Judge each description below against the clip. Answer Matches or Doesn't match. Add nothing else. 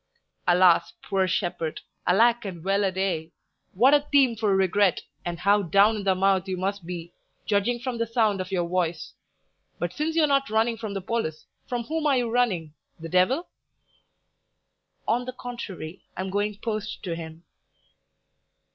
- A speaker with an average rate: Matches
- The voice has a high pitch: Matches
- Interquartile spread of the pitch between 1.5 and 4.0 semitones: Doesn't match